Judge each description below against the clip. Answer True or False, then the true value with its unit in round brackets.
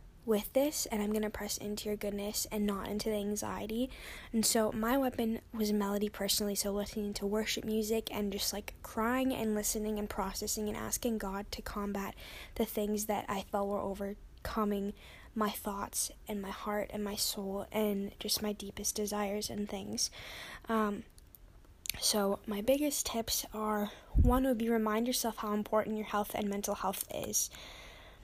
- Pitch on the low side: False (210 Hz)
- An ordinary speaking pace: True (170 wpm)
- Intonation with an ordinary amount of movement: False (1.3 semitones)